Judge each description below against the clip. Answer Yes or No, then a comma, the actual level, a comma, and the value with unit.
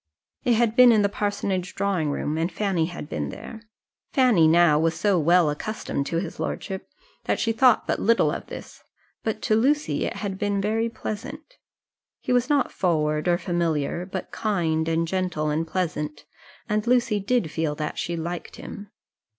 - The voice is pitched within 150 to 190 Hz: Yes, medium, 185 Hz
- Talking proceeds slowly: No, average, 175 wpm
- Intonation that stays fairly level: No, average, 5.0 semitones